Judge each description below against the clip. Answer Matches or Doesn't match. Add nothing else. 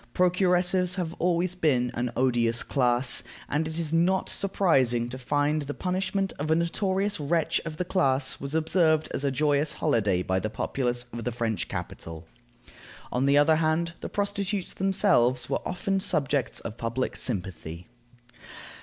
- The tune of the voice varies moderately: Doesn't match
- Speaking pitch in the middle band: Matches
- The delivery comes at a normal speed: Matches